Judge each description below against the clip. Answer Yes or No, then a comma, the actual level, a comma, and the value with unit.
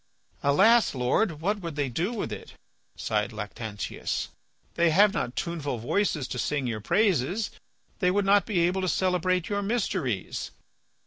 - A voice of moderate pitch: Yes, medium, 170 Hz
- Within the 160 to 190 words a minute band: No, average, 150 wpm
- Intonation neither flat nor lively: No, wide, 7.8 semitones